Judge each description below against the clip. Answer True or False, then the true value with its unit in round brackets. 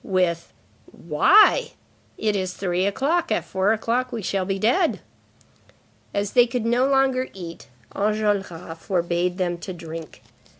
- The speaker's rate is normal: False (130 wpm)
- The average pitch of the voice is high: True (195 Hz)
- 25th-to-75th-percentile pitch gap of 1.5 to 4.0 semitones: False (5.3 semitones)